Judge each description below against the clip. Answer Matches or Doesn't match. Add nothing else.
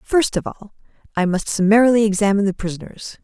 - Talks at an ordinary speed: Matches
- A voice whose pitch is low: Doesn't match